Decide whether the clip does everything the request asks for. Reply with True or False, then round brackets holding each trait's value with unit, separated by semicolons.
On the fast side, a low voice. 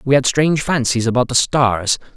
False (195 wpm; 130 Hz)